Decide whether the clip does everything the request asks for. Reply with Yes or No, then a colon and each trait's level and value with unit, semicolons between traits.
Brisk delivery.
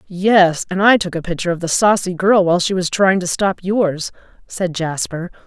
Yes: fast, 210 wpm